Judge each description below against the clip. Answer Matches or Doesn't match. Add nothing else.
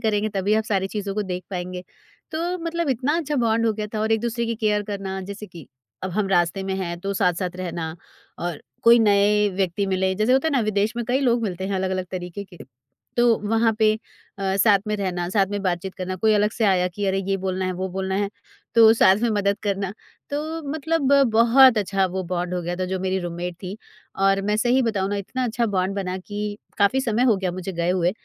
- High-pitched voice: Matches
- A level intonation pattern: Doesn't match